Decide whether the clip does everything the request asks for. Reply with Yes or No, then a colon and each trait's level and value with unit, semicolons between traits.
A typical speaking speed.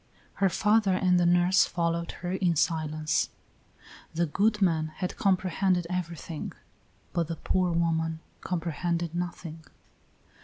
No: slow, 120 wpm